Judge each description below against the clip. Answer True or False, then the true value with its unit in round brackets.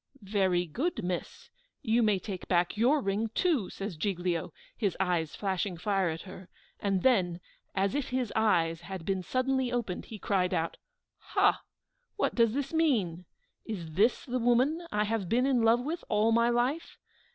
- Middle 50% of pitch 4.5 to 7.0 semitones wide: True (5.1 semitones)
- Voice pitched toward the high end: True (210 Hz)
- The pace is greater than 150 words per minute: True (170 wpm)